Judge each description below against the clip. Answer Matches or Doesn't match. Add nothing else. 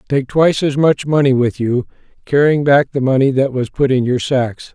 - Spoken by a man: Matches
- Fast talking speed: Matches